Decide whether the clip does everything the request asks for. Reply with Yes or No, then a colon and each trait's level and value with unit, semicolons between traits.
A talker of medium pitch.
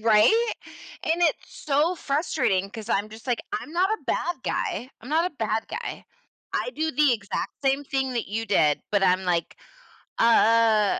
No: high, 240 Hz